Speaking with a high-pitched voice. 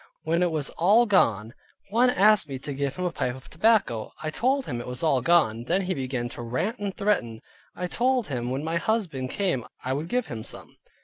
No: medium, 160 Hz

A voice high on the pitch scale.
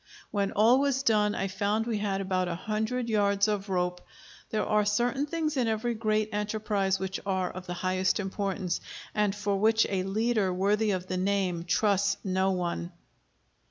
Yes: high, 200 Hz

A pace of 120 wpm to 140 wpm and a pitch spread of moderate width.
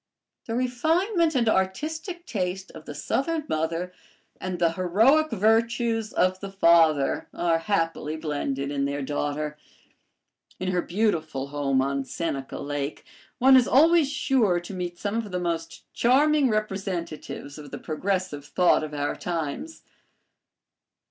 No: slow, 135 wpm; wide, 7.0 semitones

